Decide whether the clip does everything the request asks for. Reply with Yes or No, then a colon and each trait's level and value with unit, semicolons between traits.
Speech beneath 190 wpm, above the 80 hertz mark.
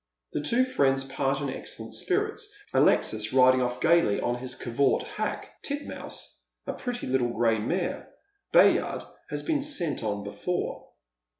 Yes: average, 140 wpm; low, 135 Hz